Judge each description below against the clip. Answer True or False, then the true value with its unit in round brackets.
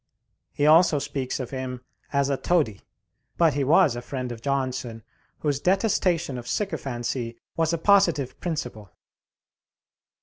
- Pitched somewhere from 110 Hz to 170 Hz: True (140 Hz)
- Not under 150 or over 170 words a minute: False (135 wpm)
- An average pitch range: True (4.6 semitones)